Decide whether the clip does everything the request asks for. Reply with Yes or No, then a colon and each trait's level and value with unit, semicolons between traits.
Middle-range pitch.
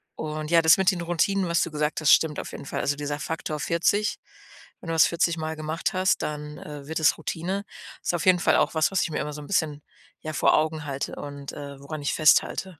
Yes: medium, 155 Hz